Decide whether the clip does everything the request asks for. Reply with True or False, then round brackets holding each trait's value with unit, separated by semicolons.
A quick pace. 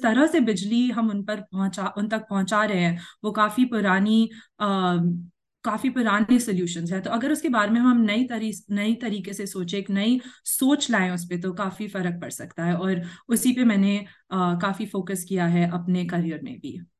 True (200 wpm)